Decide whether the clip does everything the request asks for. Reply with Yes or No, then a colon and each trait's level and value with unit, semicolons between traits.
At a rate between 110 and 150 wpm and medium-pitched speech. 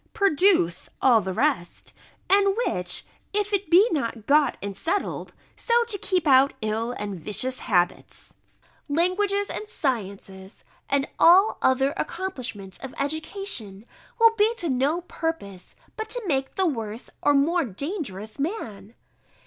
No: average, 140 wpm; very high, 280 Hz